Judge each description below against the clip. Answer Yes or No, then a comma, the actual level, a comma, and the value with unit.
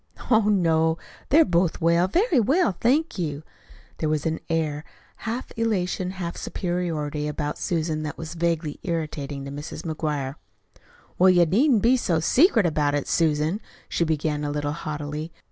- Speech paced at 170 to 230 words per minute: No, average, 155 wpm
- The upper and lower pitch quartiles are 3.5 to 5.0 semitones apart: Yes, average, 3.8 semitones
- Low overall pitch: No, medium, 165 Hz